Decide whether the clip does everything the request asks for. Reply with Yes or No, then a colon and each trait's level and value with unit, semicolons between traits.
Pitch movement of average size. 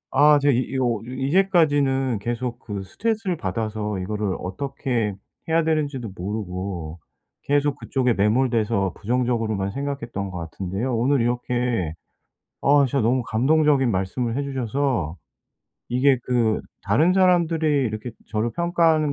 Yes: average, 5.0 semitones